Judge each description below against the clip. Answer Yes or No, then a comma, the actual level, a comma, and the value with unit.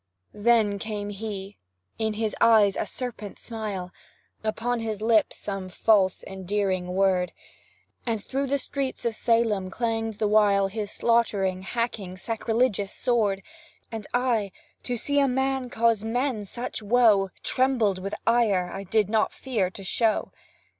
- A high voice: Yes, high, 215 Hz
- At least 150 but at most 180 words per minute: No, average, 140 wpm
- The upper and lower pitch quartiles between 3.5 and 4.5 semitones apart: No, average, 3.0 semitones